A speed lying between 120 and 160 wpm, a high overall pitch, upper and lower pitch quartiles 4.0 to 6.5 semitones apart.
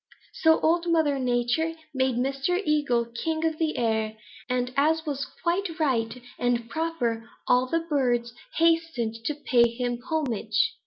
Yes: average, 145 wpm; very high, 270 Hz; average, 5.1 semitones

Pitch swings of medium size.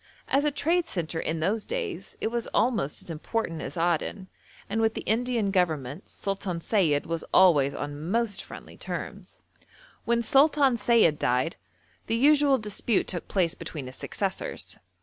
No: wide, 6.4 semitones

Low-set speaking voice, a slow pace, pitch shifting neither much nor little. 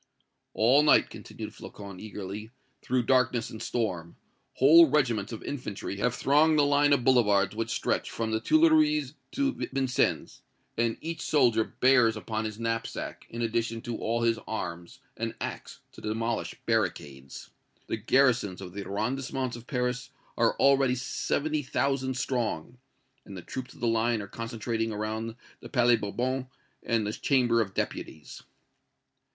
No: low, 115 Hz; average, 150 wpm; average, 3.2 semitones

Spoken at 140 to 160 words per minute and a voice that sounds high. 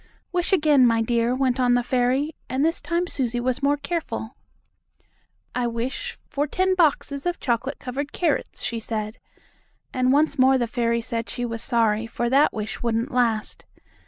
No: average, 170 wpm; very high, 250 Hz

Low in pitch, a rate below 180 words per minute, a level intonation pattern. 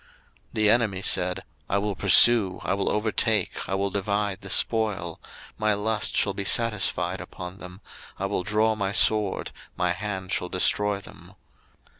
Yes: low, 100 Hz; average, 160 wpm; narrow, 2.1 semitones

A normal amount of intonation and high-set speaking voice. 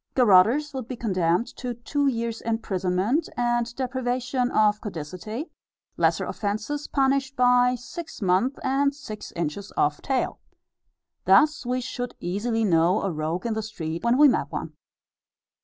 Yes: average, 4.7 semitones; high, 235 Hz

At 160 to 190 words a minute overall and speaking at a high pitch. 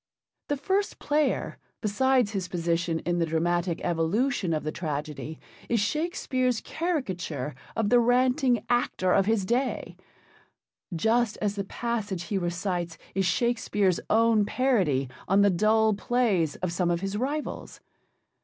No: slow, 135 wpm; high, 205 Hz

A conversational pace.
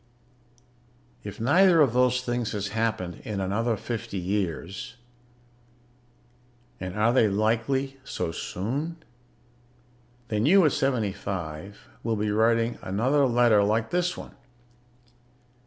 No: slow, 115 wpm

